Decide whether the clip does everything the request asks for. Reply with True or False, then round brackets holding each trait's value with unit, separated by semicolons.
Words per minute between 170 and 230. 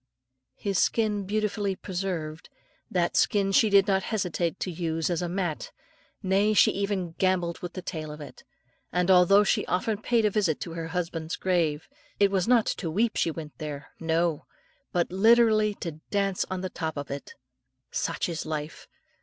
True (180 wpm)